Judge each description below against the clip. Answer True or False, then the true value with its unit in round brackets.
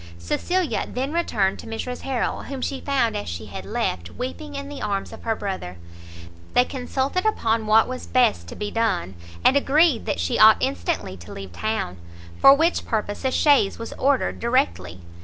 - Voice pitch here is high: True (230 Hz)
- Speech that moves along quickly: False (180 wpm)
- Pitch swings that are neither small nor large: False (6.1 semitones)